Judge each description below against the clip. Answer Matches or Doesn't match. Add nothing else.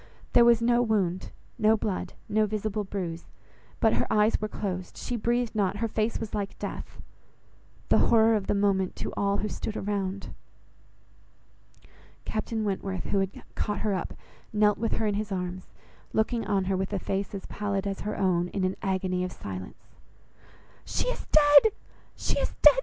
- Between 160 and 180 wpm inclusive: Matches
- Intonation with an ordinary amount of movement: Doesn't match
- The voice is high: Matches